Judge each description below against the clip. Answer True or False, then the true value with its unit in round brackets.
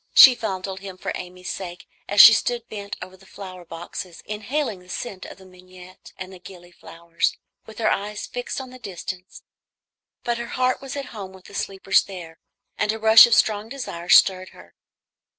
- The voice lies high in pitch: True (195 Hz)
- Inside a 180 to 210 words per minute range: True (185 wpm)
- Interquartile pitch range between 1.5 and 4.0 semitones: True (3.3 semitones)